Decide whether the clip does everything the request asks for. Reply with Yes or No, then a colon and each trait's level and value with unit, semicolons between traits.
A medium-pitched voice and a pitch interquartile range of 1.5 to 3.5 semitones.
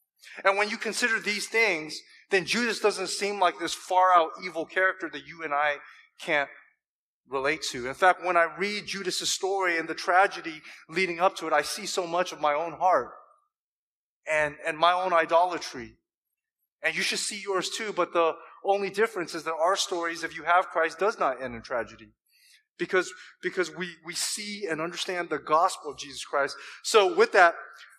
Yes: medium, 175 Hz; average, 3.1 semitones